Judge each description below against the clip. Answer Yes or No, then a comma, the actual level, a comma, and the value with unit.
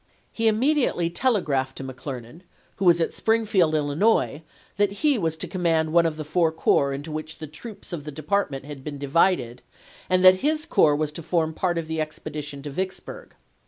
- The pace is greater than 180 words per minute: Yes, average, 190 wpm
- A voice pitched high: No, medium, 160 Hz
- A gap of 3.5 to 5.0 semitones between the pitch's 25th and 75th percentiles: Yes, average, 4.3 semitones